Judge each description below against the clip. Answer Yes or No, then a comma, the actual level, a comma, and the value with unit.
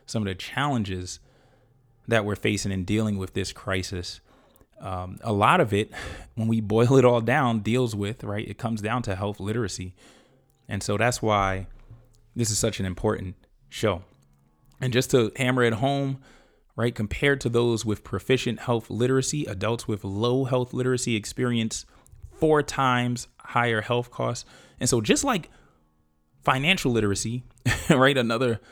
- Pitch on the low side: Yes, low, 115 Hz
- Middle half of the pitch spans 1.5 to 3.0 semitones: No, average, 3.9 semitones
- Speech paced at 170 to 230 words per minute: No, average, 155 wpm